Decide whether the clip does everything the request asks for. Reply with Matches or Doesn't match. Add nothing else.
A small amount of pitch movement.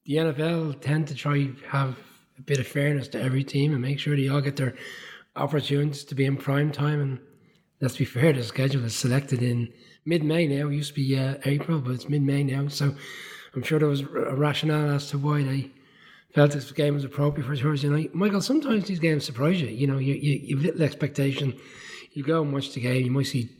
Matches